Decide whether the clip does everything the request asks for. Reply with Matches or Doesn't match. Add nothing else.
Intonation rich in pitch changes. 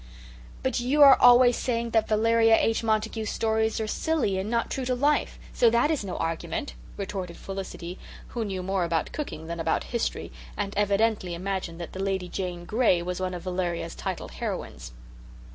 Doesn't match